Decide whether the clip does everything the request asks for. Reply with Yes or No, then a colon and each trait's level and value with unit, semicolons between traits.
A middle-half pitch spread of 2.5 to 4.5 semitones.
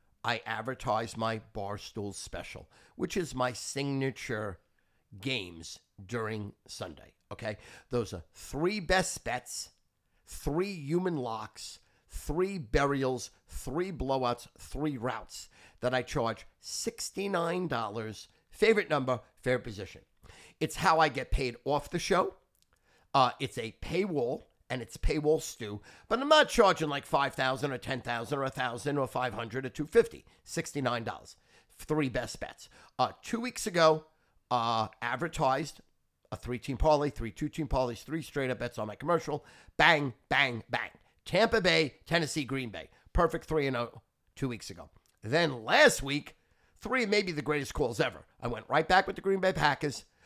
No: wide, 5.5 semitones